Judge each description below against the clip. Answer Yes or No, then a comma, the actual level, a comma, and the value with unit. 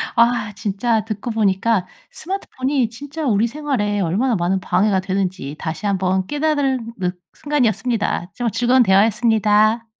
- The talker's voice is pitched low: No, high, 220 Hz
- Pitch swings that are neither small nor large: Yes, average, 4.2 semitones